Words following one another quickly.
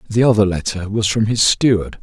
Yes: fast, 210 wpm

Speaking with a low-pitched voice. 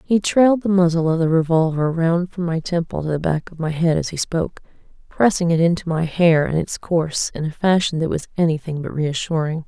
No: medium, 165 Hz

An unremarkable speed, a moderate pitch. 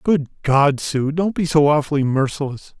Yes: average, 150 wpm; medium, 150 Hz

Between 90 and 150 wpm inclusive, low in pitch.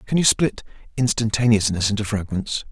Yes: slow, 135 wpm; low, 110 Hz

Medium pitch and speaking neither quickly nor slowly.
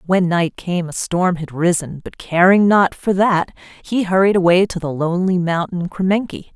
Yes: medium, 180 Hz; average, 185 wpm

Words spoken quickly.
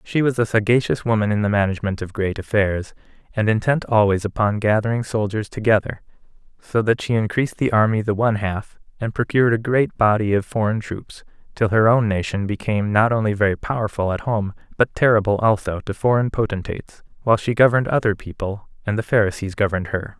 No: average, 185 wpm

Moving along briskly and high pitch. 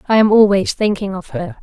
Yes: fast, 220 wpm; high, 195 Hz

